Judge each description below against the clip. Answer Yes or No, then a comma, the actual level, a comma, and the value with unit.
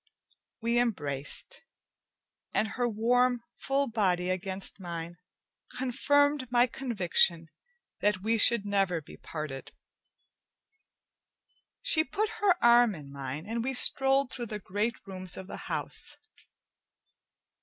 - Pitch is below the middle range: No, high, 220 Hz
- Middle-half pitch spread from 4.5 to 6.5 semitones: Yes, wide, 5.5 semitones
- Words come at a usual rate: No, slow, 115 wpm